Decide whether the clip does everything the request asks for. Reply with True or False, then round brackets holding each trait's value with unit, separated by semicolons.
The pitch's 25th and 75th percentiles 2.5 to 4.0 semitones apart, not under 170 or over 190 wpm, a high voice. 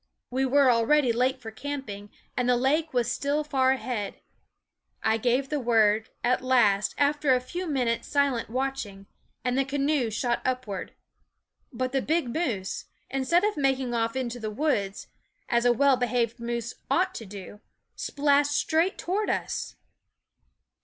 False (3.4 semitones; 155 wpm; 255 Hz)